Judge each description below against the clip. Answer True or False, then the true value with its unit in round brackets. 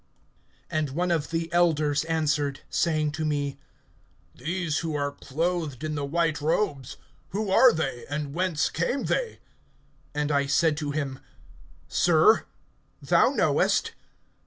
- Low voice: False (155 Hz)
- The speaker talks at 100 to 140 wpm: True (135 wpm)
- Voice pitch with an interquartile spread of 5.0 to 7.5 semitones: False (2.6 semitones)